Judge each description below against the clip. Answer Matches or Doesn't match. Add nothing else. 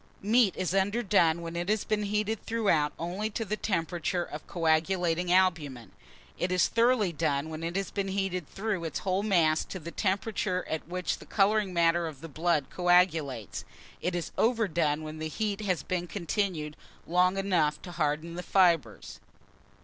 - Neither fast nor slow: Matches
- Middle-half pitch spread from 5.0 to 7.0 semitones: Doesn't match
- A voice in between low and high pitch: Matches